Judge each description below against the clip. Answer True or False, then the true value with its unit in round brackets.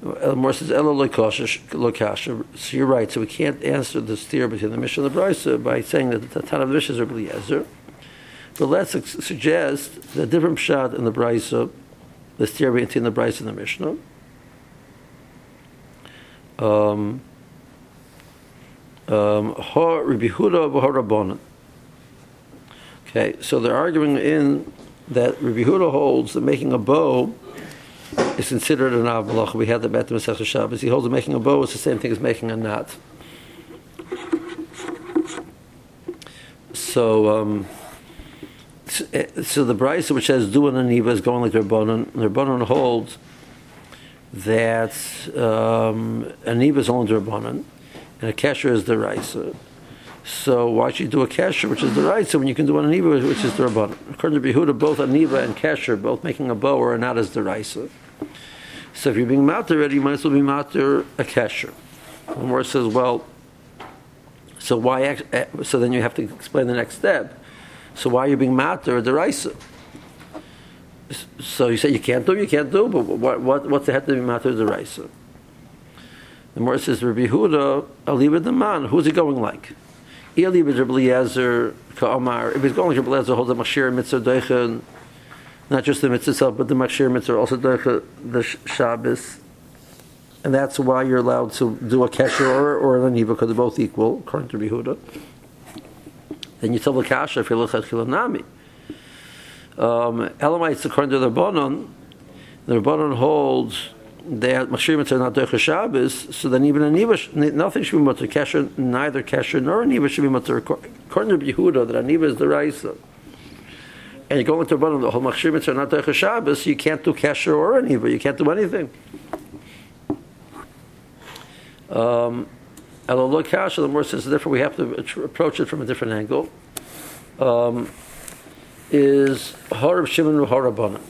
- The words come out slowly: False (160 wpm)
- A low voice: True (130 Hz)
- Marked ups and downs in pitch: False (3.7 semitones)